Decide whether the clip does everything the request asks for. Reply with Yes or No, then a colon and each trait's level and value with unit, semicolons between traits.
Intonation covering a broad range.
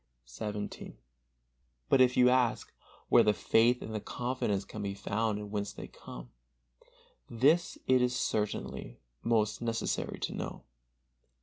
No: average, 3.2 semitones